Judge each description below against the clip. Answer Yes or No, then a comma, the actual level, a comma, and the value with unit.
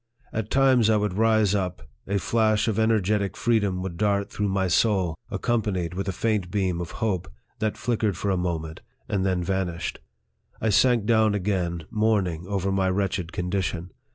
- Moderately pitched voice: No, low, 100 Hz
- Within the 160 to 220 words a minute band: Yes, average, 170 wpm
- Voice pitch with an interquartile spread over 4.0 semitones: No, average, 3.1 semitones